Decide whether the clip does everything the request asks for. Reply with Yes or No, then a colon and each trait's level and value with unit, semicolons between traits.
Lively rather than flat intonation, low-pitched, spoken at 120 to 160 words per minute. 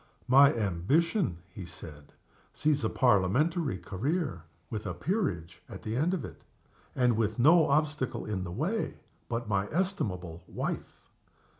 Yes: wide, 8.7 semitones; low, 115 Hz; average, 140 wpm